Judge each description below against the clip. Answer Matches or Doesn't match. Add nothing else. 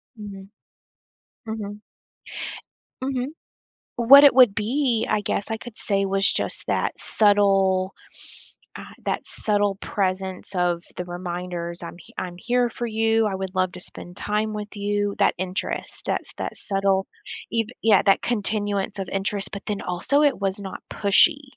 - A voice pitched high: Matches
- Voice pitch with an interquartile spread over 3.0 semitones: Doesn't match